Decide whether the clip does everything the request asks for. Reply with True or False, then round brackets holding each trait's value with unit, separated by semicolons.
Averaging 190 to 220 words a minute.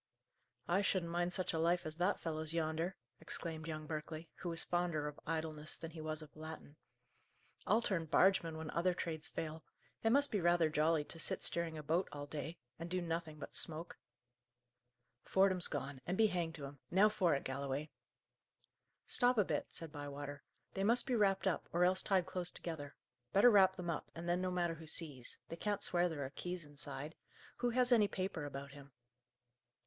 True (195 wpm)